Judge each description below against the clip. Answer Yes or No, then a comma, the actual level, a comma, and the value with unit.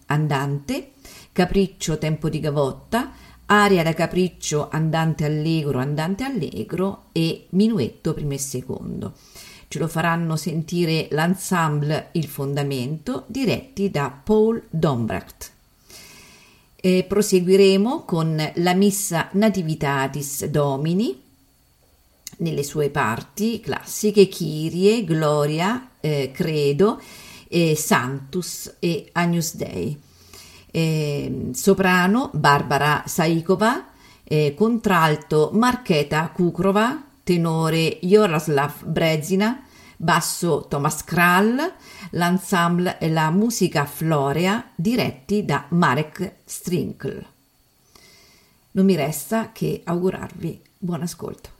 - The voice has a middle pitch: Yes, medium, 165 Hz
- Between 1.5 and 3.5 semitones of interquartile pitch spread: No, average, 4.8 semitones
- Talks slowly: Yes, slow, 85 wpm